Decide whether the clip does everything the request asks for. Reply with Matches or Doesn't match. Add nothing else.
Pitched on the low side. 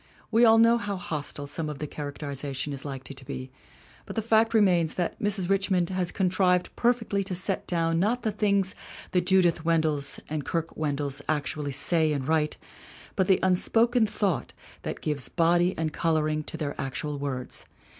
Doesn't match